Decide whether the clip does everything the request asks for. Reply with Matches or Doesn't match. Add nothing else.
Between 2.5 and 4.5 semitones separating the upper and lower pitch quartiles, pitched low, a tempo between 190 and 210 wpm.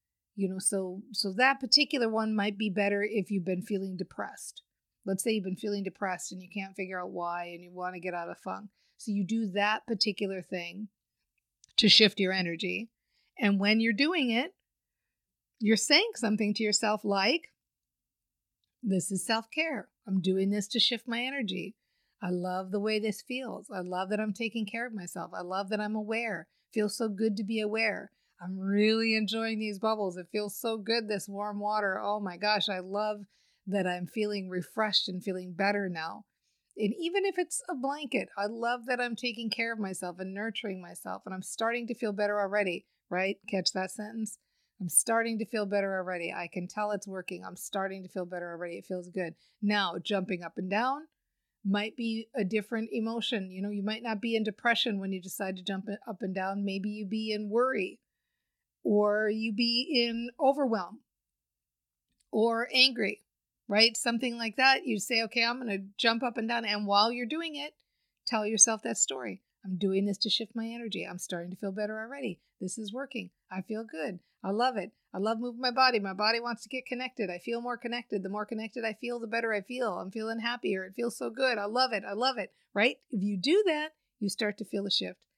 Doesn't match